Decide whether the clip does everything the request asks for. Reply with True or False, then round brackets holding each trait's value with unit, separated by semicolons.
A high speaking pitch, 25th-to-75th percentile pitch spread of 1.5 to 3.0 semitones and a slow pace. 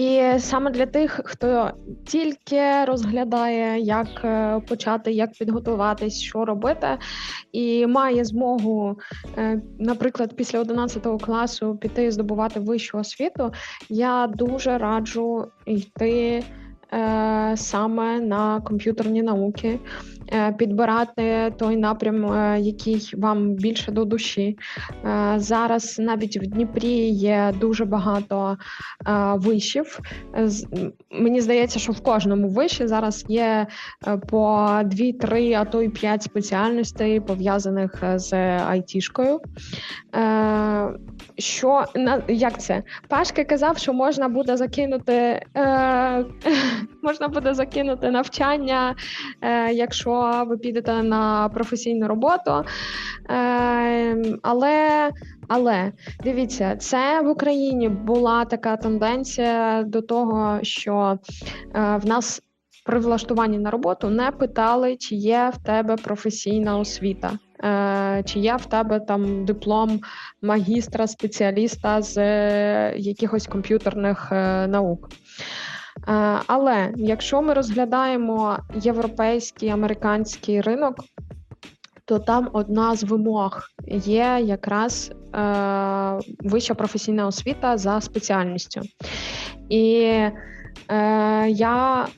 True (225 Hz; 2.4 semitones; 95 wpm)